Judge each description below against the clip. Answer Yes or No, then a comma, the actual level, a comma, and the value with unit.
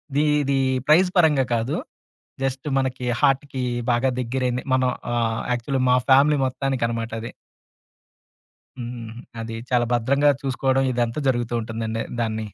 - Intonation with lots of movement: No, narrow, 2.6 semitones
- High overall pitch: No, low, 125 Hz